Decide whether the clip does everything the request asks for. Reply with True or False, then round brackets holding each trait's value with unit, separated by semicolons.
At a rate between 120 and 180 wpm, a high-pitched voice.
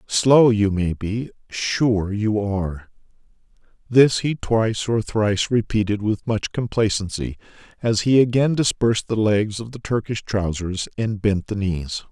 False (150 wpm; 105 Hz)